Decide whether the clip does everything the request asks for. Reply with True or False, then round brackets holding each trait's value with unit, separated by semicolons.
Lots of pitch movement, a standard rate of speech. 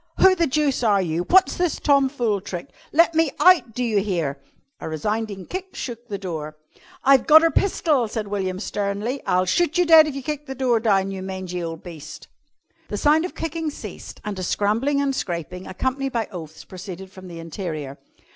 True (7.4 semitones; 190 wpm)